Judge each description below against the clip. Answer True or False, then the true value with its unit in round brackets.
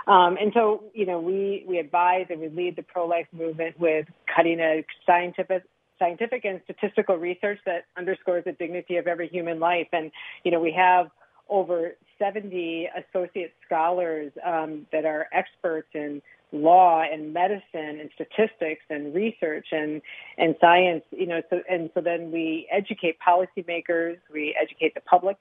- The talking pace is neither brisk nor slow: True (160 wpm)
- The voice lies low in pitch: False (175 Hz)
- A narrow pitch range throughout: True (2.1 semitones)